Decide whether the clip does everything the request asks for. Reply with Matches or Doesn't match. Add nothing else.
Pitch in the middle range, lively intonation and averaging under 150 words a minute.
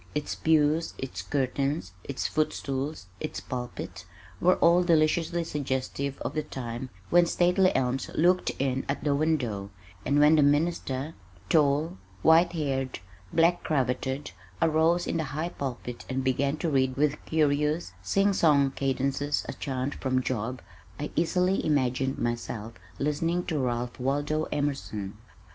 Doesn't match